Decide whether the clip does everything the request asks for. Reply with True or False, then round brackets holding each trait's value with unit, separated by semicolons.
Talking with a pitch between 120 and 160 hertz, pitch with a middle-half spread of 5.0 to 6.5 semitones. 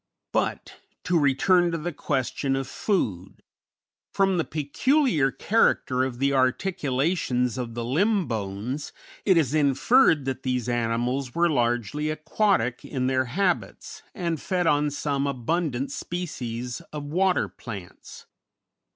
True (140 Hz; 5.5 semitones)